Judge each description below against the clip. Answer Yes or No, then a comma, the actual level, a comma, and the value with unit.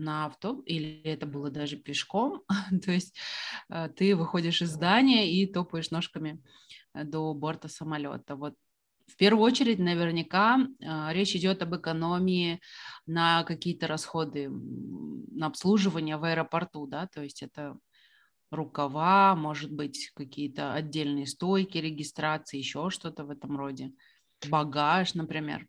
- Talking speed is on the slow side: No, average, 125 wpm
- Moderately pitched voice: Yes, medium, 160 Hz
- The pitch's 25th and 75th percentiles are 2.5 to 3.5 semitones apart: Yes, average, 3.1 semitones